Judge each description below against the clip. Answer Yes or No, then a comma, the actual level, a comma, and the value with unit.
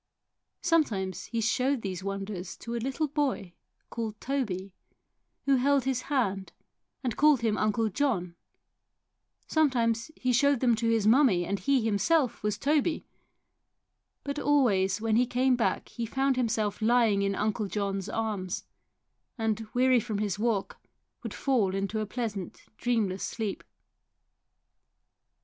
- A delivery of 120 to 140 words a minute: Yes, slow, 135 wpm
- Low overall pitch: No, high, 225 Hz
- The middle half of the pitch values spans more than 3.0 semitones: Yes, average, 4.5 semitones